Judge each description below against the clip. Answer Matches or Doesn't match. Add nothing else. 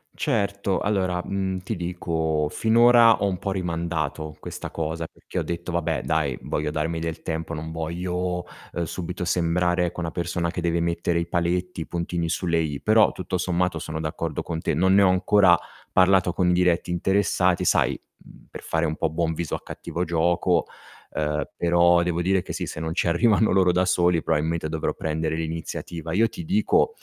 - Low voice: Matches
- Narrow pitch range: Matches